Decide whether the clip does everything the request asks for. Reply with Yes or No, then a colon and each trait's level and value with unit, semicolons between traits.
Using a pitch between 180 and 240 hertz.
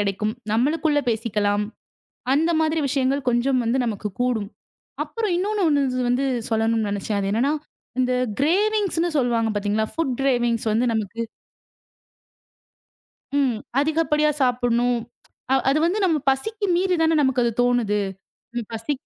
No: very high, 250 Hz